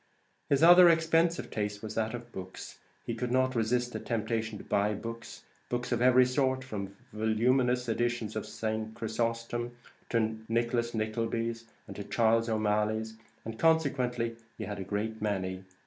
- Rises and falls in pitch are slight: Yes, narrow, 2.1 semitones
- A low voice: Yes, low, 115 Hz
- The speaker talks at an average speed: Yes, average, 150 wpm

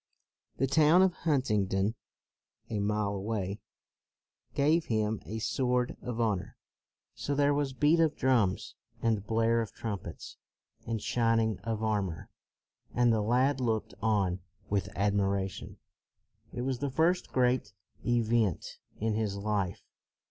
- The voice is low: Yes, low, 115 Hz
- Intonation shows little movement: No, average, 4.0 semitones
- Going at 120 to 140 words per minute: Yes, slow, 135 wpm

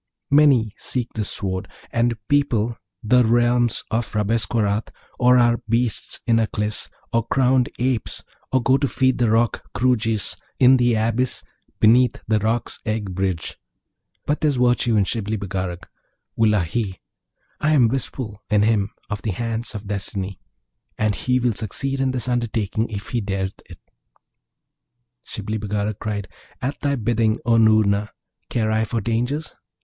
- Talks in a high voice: No, low, 115 Hz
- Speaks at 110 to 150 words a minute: Yes, average, 145 wpm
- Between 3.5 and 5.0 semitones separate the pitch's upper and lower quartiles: No, average, 2.7 semitones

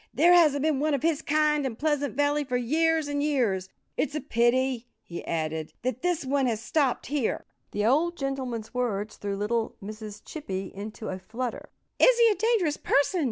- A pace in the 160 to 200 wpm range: Yes, average, 185 wpm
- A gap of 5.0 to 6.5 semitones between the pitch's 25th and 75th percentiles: Yes, wide, 5.4 semitones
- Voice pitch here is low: No, very high, 265 Hz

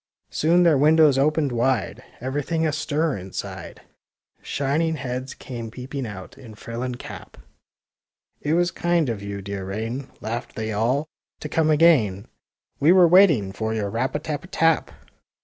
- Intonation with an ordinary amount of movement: No, wide, 5.9 semitones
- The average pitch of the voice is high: No, low, 135 Hz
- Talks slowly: No, average, 165 wpm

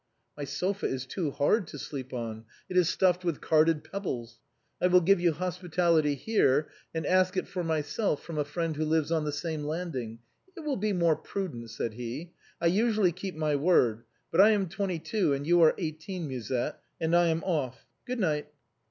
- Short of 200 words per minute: No, fast, 205 wpm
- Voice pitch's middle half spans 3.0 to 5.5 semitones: Yes, average, 4.0 semitones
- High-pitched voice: No, medium, 165 Hz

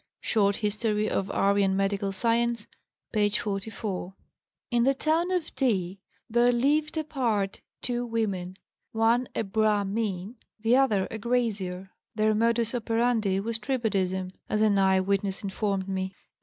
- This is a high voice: Yes, high, 215 Hz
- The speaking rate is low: Yes, slow, 130 wpm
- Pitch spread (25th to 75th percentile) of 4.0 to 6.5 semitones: No, average, 3.3 semitones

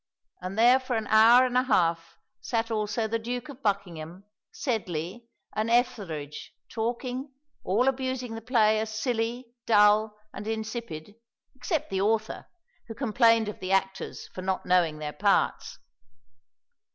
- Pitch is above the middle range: Yes, high, 220 Hz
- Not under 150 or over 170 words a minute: No, average, 140 wpm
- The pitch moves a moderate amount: Yes, average, 3.9 semitones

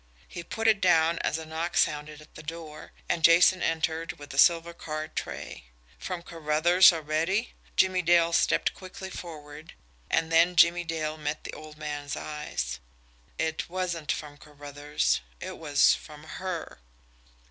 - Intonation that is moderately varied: No, narrow, 2.2 semitones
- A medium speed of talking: Yes, average, 150 wpm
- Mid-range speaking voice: Yes, medium, 160 Hz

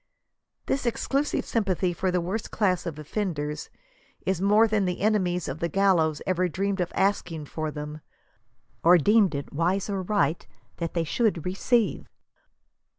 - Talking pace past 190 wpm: No, average, 155 wpm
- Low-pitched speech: No, medium, 185 Hz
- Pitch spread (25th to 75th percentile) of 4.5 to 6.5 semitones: No, average, 3.6 semitones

